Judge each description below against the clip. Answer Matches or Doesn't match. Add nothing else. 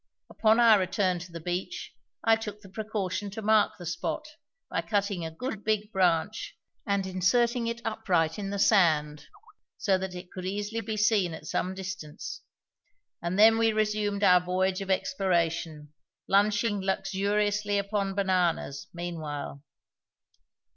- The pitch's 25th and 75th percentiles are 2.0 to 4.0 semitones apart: Matches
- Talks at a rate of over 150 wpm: Doesn't match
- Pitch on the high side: Matches